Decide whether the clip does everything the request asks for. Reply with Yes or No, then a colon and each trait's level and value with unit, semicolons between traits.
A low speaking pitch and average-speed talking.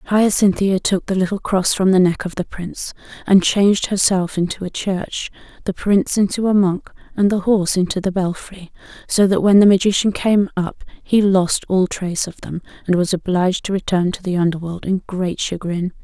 No: high, 190 Hz; average, 195 wpm